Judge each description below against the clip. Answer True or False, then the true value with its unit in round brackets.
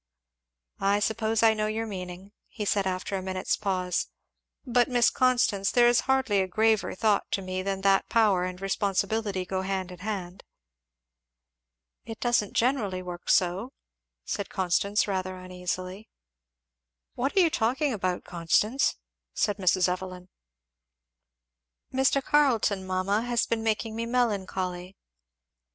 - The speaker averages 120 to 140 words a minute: True (135 wpm)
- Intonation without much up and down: False (3.4 semitones)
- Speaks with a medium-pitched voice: False (200 Hz)